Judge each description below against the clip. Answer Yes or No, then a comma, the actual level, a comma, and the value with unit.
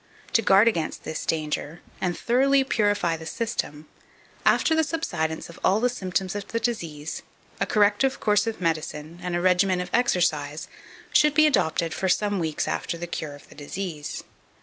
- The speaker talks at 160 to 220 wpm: Yes, average, 170 wpm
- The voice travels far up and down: Yes, wide, 5.9 semitones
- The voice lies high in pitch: No, medium, 180 Hz